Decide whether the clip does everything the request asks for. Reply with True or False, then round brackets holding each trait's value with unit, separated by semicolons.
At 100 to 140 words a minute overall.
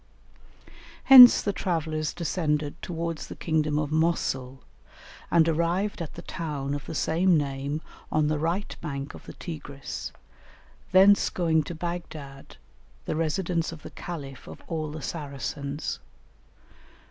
True (135 wpm)